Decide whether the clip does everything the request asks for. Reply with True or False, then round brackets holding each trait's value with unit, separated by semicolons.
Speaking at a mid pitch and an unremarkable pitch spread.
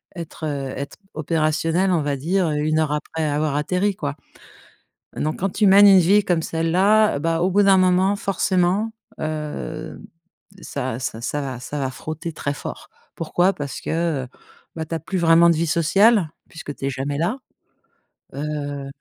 True (160 Hz; 3.7 semitones)